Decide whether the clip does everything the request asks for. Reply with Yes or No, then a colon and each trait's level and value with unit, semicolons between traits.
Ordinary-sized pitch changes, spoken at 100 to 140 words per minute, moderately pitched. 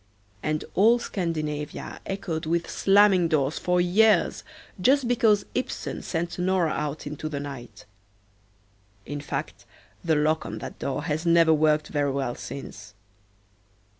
Yes: average, 3.8 semitones; slow, 135 wpm; medium, 160 Hz